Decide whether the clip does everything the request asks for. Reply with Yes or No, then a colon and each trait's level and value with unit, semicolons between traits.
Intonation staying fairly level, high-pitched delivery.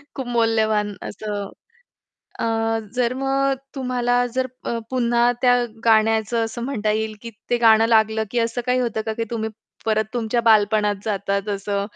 Yes: narrow, 2.0 semitones; high, 225 Hz